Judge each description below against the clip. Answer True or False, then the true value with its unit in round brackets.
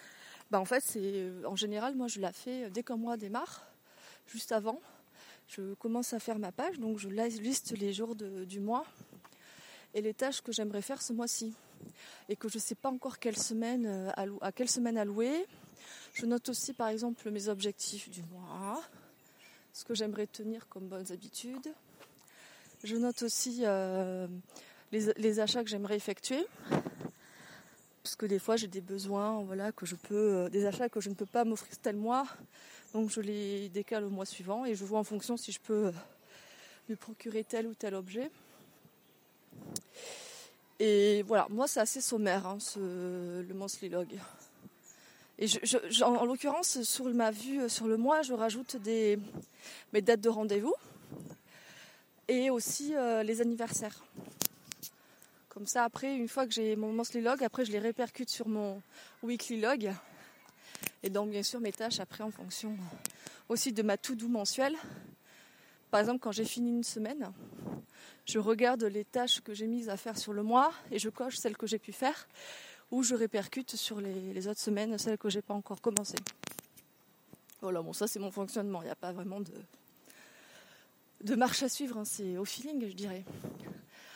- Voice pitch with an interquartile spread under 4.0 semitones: True (2.8 semitones)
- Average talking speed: True (175 wpm)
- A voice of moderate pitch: False (220 Hz)